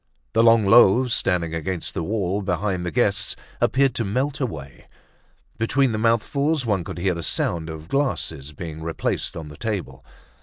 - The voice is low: Yes, very low, 95 Hz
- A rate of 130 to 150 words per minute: No, average, 165 wpm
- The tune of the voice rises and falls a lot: Yes, wide, 6.1 semitones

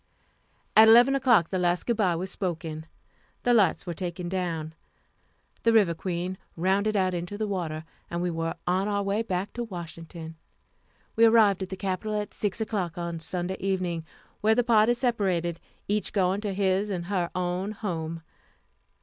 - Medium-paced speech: Yes, average, 170 wpm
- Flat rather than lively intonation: No, average, 3.4 semitones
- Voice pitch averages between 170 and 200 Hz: Yes, medium, 185 Hz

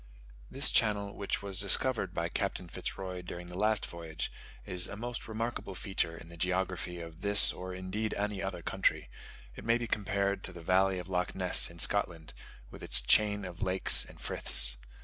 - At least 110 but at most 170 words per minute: No, average, 190 wpm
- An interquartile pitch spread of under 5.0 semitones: Yes, narrow, 2.6 semitones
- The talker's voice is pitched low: Yes, very low, 95 Hz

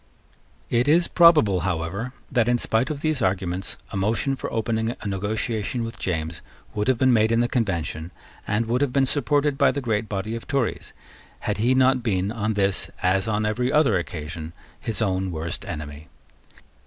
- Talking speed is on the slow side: No, average, 180 wpm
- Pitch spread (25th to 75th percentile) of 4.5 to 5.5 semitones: Yes, average, 4.8 semitones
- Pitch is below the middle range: Yes, low, 110 Hz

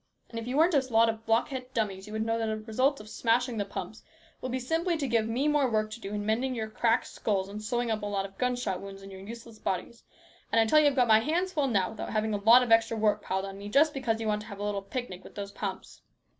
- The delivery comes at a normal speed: No, fast, 290 wpm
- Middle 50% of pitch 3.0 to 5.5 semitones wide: Yes, average, 3.3 semitones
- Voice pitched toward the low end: No, high, 225 Hz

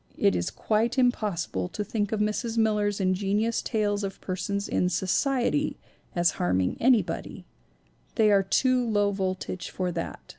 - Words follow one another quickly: No, average, 145 wpm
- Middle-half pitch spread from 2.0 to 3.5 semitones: Yes, average, 3.2 semitones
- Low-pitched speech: No, high, 205 Hz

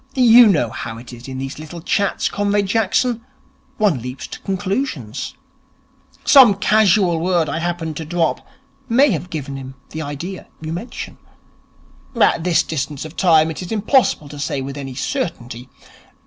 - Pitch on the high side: No, medium, 165 Hz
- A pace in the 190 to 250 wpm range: No, average, 160 wpm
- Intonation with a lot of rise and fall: Yes, wide, 6.1 semitones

